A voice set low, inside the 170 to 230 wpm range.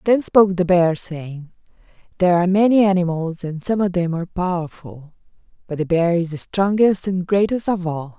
No: medium, 180 Hz; average, 185 wpm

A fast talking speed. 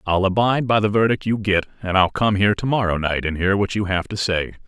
Yes: fast, 270 wpm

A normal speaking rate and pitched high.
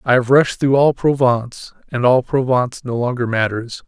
No: average, 170 wpm; low, 125 Hz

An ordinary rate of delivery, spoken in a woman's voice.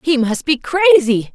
Yes: average, 180 wpm; female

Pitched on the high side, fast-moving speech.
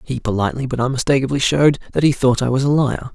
No: low, 130 Hz; fast, 230 wpm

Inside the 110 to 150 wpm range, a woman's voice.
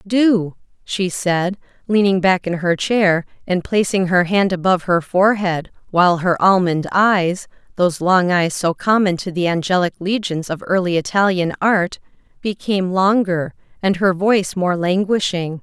Yes: average, 140 wpm; female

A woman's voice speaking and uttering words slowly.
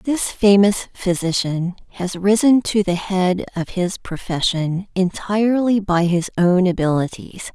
Yes: female; slow, 125 wpm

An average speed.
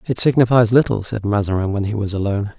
No: fast, 210 wpm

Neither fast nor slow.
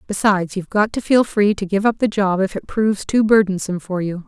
No: fast, 255 wpm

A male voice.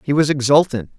Yes: male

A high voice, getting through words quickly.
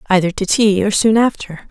Yes: high, 200 Hz; fast, 210 wpm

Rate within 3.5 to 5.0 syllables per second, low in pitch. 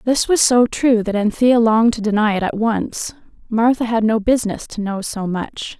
No: 4.9 syllables/s; high, 225 Hz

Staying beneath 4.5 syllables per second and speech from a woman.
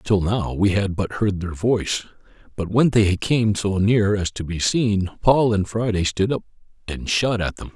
No: 4.3 syllables/s; male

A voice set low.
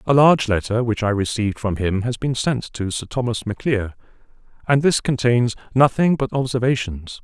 Yes: low, 120 Hz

